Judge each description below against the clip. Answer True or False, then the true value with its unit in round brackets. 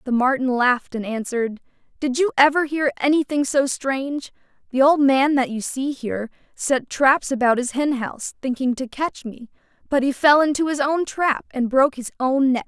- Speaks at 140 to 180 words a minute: False (195 wpm)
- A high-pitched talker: True (265 Hz)